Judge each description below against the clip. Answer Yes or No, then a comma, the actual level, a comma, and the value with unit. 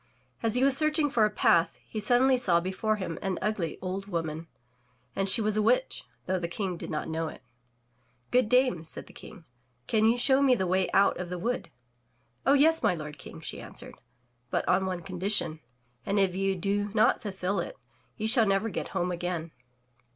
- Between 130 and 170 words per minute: No, average, 200 wpm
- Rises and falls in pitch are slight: No, average, 4.4 semitones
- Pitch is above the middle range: Yes, high, 195 Hz